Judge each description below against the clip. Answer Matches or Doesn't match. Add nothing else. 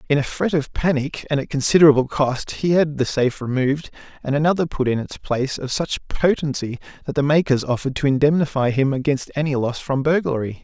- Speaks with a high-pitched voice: Doesn't match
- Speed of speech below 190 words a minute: Doesn't match